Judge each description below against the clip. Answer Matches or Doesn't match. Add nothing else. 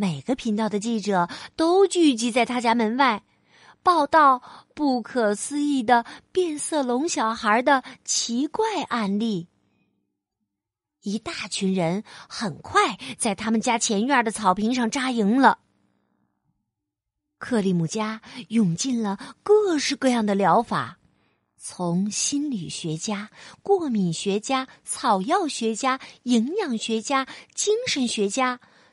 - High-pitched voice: Matches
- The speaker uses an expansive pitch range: Doesn't match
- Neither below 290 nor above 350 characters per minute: Doesn't match